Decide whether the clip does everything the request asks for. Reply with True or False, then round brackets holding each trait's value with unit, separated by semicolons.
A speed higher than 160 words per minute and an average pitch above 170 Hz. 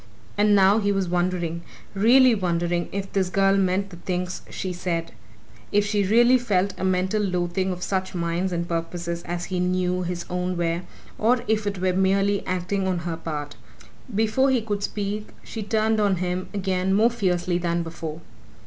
True (175 wpm; 185 Hz)